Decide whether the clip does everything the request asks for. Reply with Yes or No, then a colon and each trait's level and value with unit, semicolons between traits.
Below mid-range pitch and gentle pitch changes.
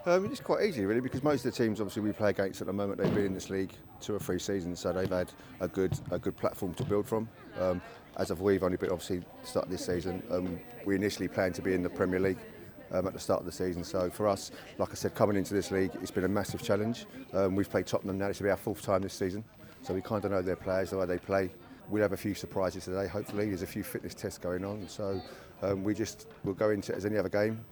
Yes: low, 100 Hz; narrow, 2.0 semitones